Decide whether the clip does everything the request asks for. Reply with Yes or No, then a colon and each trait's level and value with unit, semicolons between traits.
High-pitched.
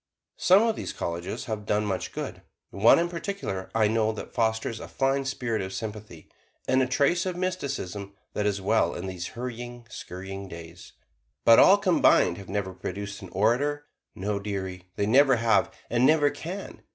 No: low, 110 Hz